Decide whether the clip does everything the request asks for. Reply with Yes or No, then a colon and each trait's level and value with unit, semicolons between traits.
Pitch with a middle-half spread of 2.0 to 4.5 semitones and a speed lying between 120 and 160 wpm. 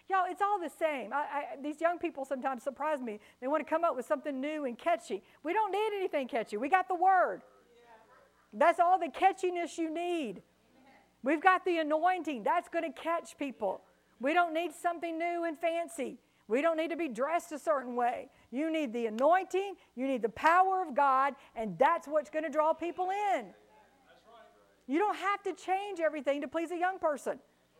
No: average, 3.9 semitones; average, 200 wpm